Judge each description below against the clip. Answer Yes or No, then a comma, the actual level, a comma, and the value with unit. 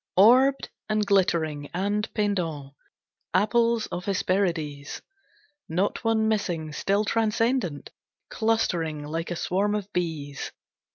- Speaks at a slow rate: Yes, slow, 105 wpm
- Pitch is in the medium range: No, high, 195 Hz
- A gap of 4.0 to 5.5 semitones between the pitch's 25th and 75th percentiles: Yes, average, 4.8 semitones